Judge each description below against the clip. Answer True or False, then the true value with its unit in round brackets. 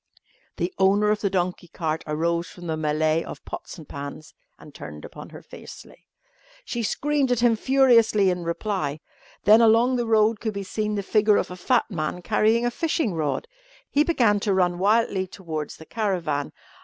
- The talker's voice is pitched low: False (200 Hz)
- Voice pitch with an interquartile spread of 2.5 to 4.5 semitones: False (5.0 semitones)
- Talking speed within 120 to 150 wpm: False (180 wpm)